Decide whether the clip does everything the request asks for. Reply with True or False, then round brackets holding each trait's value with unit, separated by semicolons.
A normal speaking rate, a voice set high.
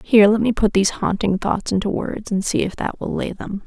False (260 wpm; 205 Hz)